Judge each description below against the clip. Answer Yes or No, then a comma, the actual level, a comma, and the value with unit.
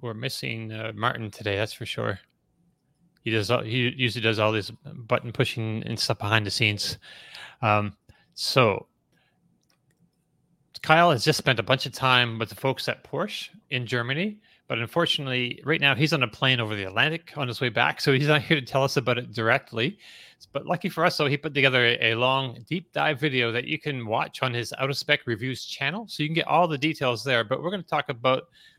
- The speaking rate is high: Yes, fast, 215 wpm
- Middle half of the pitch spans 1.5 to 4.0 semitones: No, average, 4.7 semitones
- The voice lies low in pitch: Yes, low, 130 Hz